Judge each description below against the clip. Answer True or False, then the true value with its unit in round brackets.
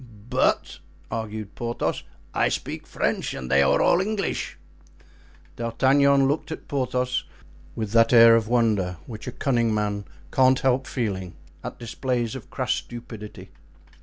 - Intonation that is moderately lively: True (3.4 semitones)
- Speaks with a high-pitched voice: False (115 Hz)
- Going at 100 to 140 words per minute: True (135 wpm)